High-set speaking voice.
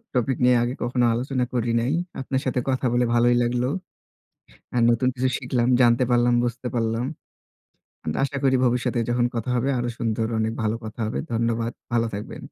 No: low, 120 Hz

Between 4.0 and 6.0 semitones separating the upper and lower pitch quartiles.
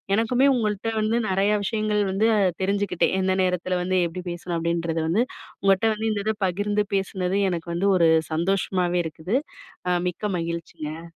No: average, 3.5 semitones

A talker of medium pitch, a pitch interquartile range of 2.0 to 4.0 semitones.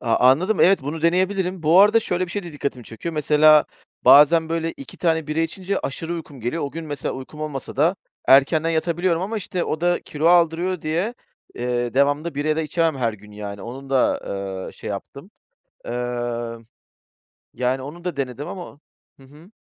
No: medium, 155 Hz; average, 4.5 semitones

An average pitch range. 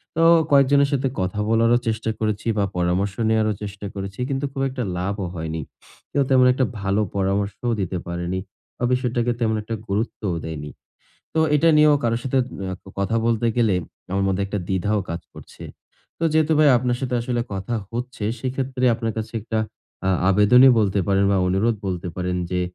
Yes: average, 4.5 semitones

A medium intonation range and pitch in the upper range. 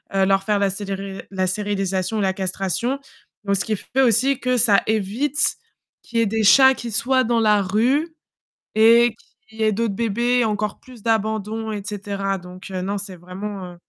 Yes: average, 3.1 semitones; high, 210 Hz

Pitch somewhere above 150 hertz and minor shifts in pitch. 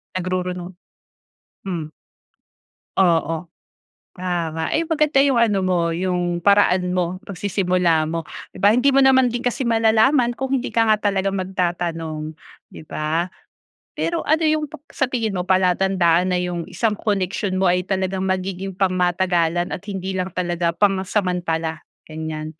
No: medium, 185 Hz; average, 3.3 semitones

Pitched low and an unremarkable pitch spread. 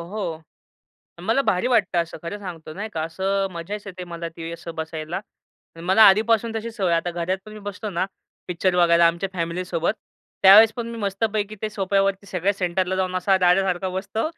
No: high, 190 Hz; average, 3.1 semitones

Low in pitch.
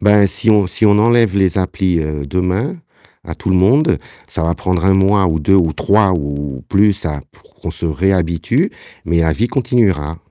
Yes: very low, 95 Hz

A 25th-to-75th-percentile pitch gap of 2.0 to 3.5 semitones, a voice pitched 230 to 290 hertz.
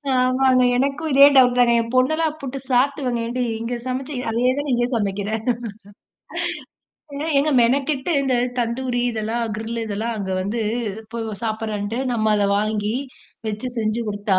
Yes: average, 3.2 semitones; high, 235 Hz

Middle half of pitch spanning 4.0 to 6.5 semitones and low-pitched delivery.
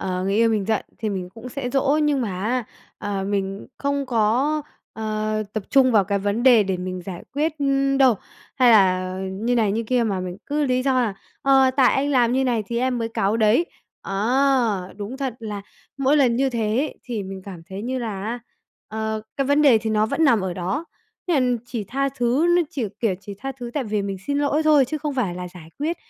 No: average, 4.9 semitones; high, 230 Hz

